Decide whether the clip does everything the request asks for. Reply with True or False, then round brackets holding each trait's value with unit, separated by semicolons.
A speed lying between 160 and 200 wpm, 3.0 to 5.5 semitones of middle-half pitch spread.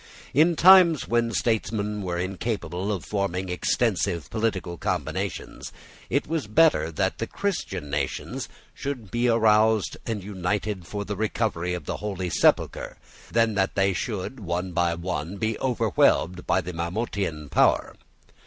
False (140 wpm; 4.2 semitones)